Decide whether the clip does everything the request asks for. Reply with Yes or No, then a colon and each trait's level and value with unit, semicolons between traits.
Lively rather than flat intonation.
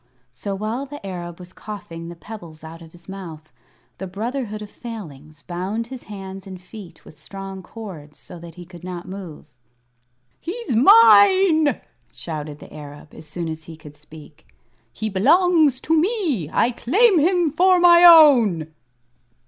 Yes: wide, 7.8 semitones